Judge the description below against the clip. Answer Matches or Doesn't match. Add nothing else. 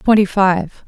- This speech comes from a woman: Matches